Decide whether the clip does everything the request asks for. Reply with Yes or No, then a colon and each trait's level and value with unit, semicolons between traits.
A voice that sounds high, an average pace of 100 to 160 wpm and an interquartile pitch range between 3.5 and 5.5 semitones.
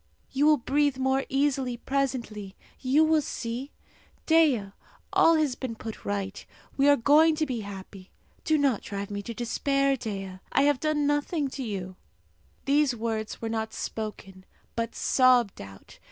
Yes: very high, 255 Hz; average, 155 wpm; average, 4.9 semitones